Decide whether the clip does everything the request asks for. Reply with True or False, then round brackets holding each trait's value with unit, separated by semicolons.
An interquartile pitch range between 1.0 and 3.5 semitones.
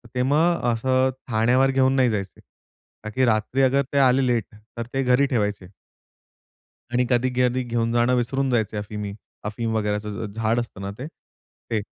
True (3.1 semitones)